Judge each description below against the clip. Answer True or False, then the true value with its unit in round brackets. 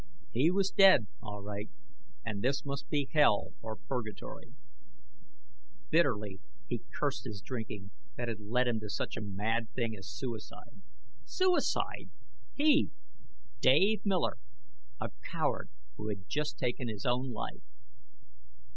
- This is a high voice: False (115 Hz)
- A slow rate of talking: True (130 wpm)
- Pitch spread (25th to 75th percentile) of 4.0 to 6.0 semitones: True (5.1 semitones)